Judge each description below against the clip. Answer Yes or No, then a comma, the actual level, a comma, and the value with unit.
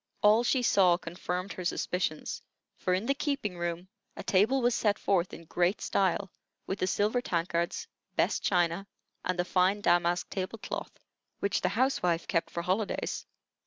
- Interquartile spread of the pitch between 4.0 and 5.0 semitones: No, average, 3.1 semitones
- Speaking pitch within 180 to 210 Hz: Yes, medium, 185 Hz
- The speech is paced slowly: No, average, 160 wpm